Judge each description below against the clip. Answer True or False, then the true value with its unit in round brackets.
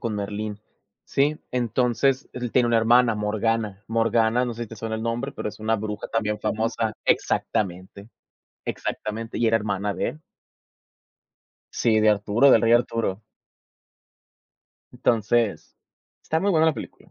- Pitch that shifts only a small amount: True (2.1 semitones)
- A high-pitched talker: False (115 Hz)